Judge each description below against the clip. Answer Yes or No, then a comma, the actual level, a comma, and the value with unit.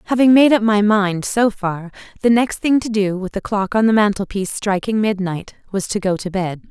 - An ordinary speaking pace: No, fast, 235 wpm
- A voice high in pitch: Yes, high, 205 Hz